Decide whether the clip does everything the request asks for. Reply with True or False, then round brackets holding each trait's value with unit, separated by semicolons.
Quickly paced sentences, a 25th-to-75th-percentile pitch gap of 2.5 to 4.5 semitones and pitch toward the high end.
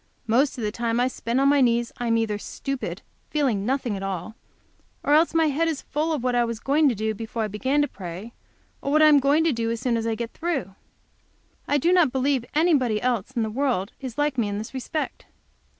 True (230 wpm; 4.2 semitones; 250 Hz)